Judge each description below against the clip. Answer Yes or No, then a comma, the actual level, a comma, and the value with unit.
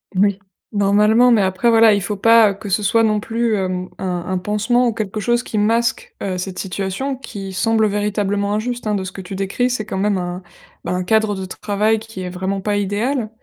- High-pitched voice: Yes, high, 205 Hz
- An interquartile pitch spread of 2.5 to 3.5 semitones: Yes, average, 2.8 semitones